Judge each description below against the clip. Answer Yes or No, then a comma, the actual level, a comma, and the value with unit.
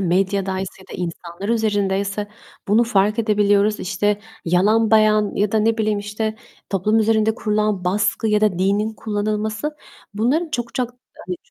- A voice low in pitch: No, high, 210 Hz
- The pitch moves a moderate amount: No, narrow, 1.8 semitones